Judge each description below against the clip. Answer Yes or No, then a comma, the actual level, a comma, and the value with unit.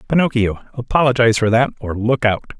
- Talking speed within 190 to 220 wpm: No, average, 160 wpm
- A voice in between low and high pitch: No, low, 120 Hz